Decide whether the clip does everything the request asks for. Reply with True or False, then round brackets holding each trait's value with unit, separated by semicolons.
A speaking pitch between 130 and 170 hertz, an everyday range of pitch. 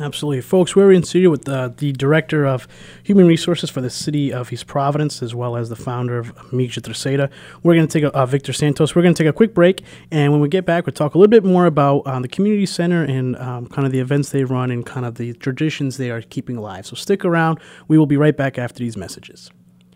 True (140 Hz; 4.6 semitones)